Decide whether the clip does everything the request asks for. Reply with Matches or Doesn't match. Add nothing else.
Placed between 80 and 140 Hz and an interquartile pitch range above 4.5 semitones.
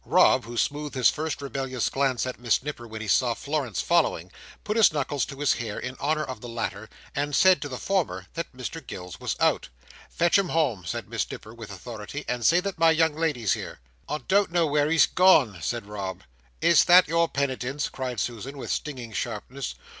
Matches